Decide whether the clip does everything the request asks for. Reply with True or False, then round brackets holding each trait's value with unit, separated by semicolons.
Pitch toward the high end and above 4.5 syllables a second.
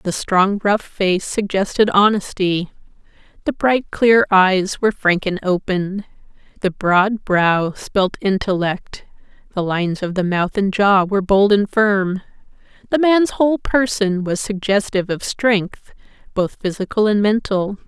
False (200 Hz; 4.1 syllables/s)